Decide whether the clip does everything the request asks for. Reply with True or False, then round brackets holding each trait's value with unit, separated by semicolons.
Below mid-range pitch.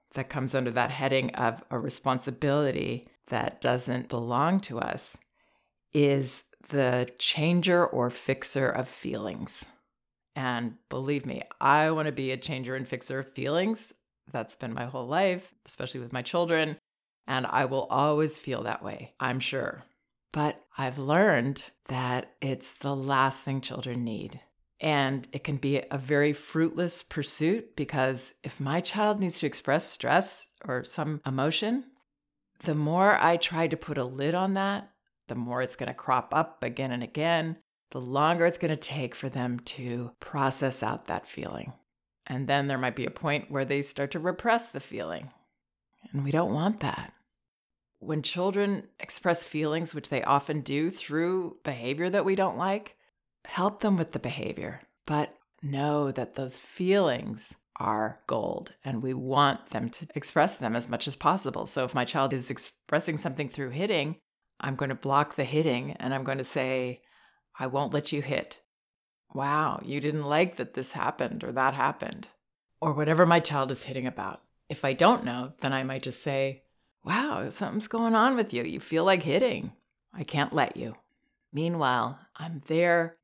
False (145 Hz)